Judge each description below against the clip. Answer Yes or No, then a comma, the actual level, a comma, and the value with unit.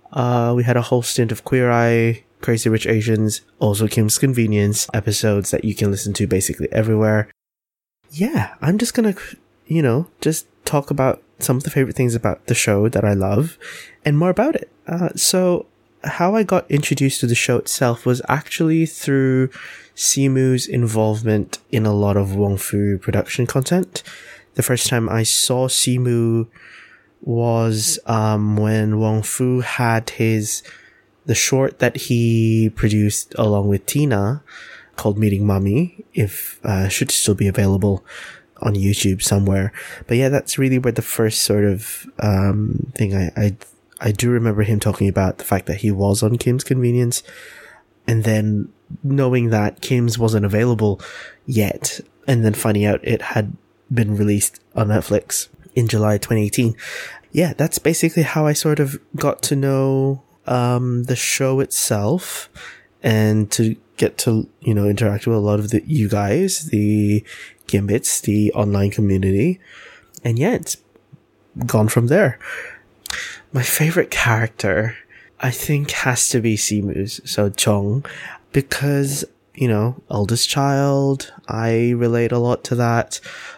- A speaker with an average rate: Yes, average, 150 wpm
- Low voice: Yes, low, 115 Hz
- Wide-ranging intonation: No, average, 4.1 semitones